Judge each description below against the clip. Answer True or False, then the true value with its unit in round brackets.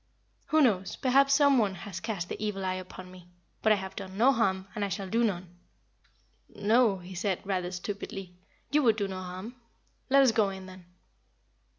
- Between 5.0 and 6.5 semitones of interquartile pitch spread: False (3.4 semitones)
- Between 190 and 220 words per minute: True (195 wpm)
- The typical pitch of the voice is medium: False (195 Hz)